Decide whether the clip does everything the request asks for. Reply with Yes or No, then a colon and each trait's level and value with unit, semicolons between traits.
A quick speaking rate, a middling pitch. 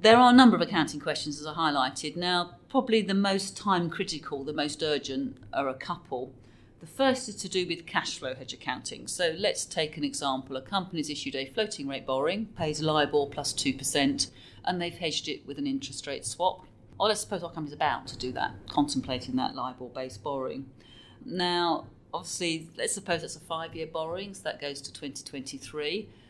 No: average, 195 wpm; medium, 150 Hz